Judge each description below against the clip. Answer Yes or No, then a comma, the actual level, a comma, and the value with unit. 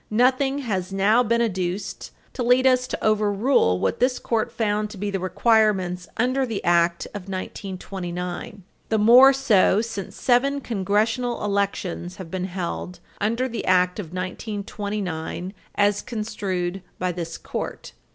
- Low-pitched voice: No, high, 205 Hz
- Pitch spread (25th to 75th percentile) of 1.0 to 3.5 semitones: No, average, 4.1 semitones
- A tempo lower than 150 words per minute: Yes, average, 140 wpm